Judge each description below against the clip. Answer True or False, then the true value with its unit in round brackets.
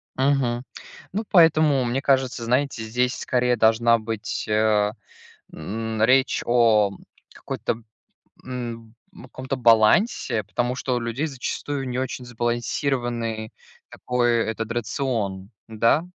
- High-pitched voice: False (120 Hz)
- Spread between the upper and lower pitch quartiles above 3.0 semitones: False (2.6 semitones)